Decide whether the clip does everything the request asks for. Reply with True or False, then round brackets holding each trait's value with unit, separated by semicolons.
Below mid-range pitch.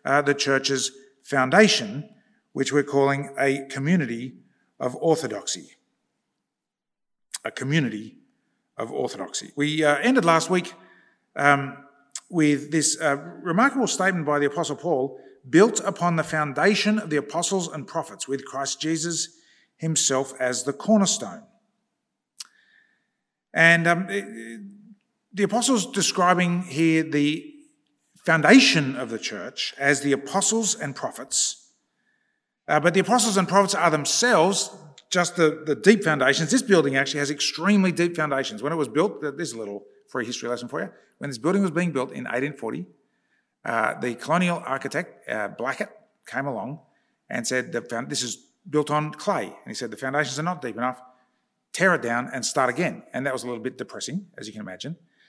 False (160 Hz)